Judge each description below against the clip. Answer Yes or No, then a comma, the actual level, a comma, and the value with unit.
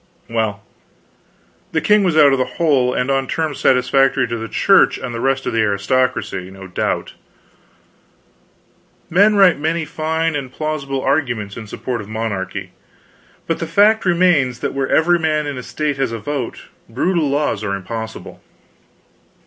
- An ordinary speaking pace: Yes, average, 160 wpm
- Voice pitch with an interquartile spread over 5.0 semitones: Yes, wide, 5.6 semitones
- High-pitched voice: No, low, 135 Hz